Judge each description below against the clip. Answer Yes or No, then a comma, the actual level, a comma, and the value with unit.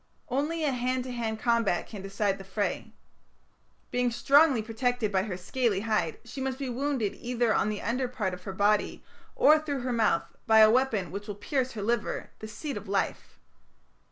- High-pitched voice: Yes, high, 230 Hz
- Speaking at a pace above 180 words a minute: Yes, average, 190 wpm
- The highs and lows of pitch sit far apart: No, average, 3.8 semitones